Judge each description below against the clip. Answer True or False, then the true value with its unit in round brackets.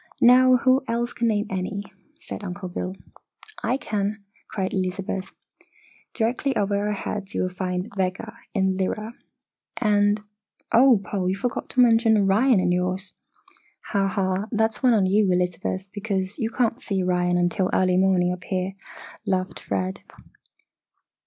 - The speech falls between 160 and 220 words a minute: False (145 wpm)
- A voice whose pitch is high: True (195 Hz)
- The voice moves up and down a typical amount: True (3.1 semitones)